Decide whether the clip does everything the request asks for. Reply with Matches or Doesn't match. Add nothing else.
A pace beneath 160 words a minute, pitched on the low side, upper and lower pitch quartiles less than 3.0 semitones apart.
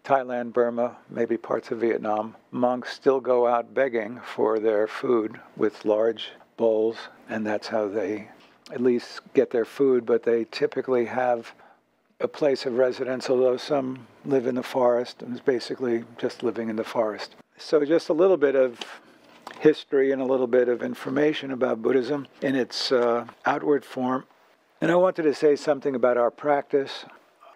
Doesn't match